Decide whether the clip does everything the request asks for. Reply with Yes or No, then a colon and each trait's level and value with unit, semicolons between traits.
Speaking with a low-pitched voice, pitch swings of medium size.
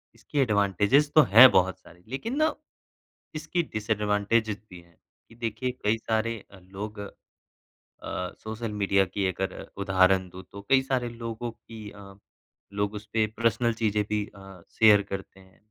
Yes: low, 105 Hz; average, 3.1 semitones